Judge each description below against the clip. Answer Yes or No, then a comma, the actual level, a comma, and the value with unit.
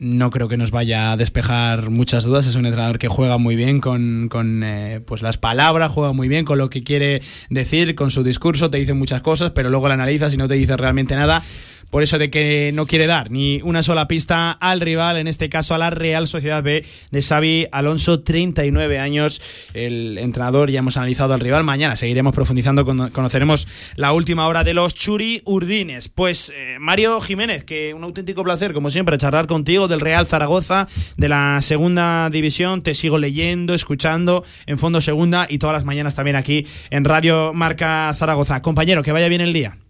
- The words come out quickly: Yes, fast, 200 wpm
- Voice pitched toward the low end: No, medium, 150 Hz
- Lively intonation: No, average, 3.8 semitones